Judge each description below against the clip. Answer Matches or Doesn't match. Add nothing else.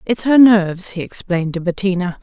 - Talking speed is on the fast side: Doesn't match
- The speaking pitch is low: Doesn't match